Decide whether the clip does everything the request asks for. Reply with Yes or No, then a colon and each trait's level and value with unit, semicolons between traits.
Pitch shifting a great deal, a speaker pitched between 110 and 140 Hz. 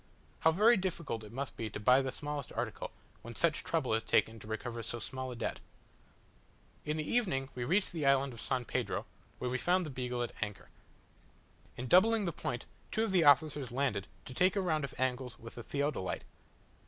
No: average, 5.0 semitones; low, 135 Hz